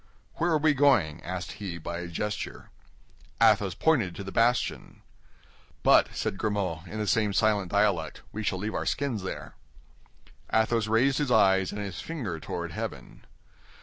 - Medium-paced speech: Yes, average, 160 wpm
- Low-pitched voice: Yes, low, 105 Hz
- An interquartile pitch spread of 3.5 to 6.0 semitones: Yes, average, 4.1 semitones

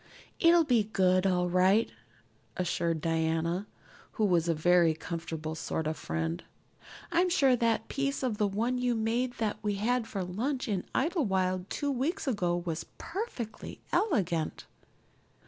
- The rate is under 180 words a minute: Yes, average, 145 wpm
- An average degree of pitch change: No, wide, 6.3 semitones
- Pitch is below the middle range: No, high, 205 Hz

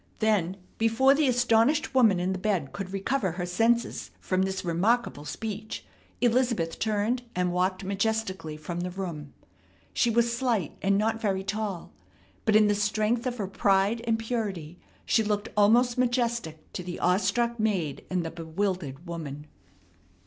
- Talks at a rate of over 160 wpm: No, average, 155 wpm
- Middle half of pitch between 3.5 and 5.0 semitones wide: Yes, average, 4.2 semitones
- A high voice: Yes, high, 205 Hz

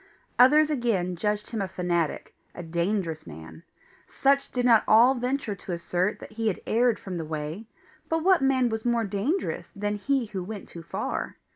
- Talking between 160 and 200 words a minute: Yes, average, 180 wpm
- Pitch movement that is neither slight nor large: No, wide, 5.8 semitones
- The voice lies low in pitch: No, high, 210 Hz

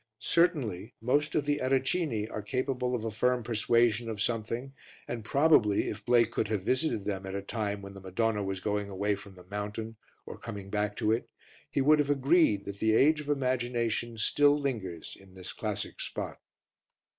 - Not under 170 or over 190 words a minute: Yes, average, 185 wpm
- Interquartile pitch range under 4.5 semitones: Yes, average, 4.1 semitones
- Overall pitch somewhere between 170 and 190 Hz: No, low, 115 Hz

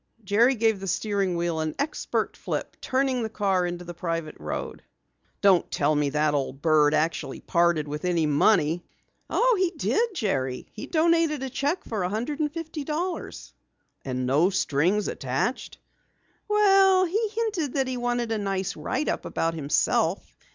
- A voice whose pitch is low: No, high, 200 Hz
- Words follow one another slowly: No, average, 165 wpm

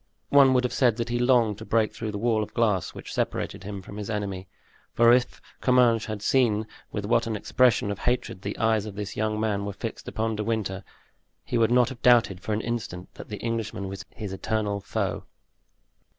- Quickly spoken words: Yes, fast, 210 wpm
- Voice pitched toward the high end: No, low, 110 Hz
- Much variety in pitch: No, narrow, 2.5 semitones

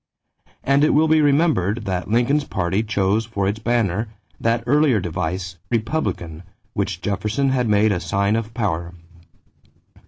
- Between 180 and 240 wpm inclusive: No, average, 145 wpm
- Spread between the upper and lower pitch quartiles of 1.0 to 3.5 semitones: No, average, 4.7 semitones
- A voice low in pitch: Yes, low, 110 Hz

